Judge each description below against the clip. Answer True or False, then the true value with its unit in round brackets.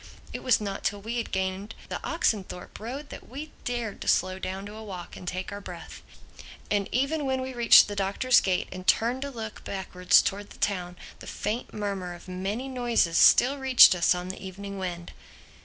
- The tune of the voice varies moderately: True (4.4 semitones)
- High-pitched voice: True (205 Hz)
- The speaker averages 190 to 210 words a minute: True (200 wpm)